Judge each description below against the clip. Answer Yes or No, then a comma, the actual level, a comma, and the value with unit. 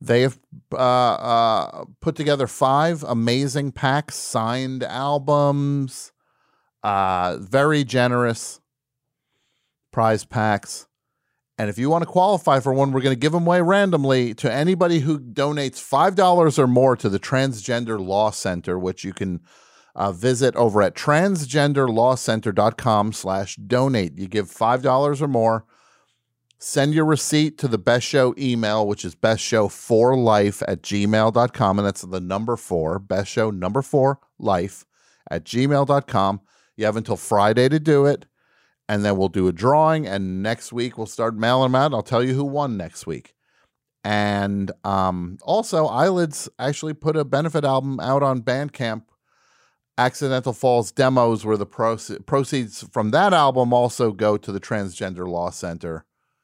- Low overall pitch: Yes, low, 125 Hz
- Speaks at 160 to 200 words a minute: No, average, 150 wpm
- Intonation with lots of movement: No, average, 5.0 semitones